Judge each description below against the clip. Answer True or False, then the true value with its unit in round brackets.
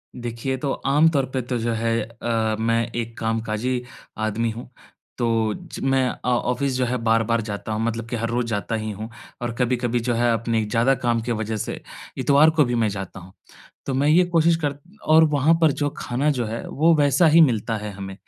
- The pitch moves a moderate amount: True (3.0 semitones)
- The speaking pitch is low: True (120 Hz)